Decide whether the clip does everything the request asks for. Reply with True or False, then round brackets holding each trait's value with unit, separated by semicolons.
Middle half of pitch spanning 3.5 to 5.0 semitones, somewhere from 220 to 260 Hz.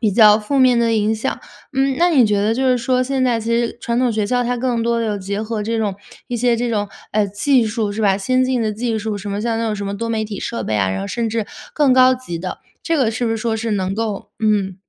False (2.9 semitones; 225 Hz)